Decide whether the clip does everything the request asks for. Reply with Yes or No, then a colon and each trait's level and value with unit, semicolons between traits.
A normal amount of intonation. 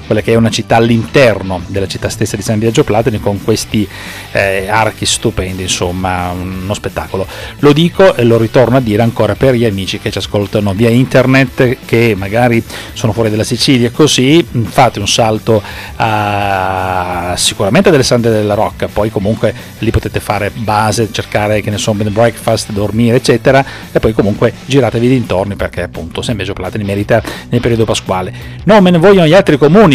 Yes: average, 3.1 semitones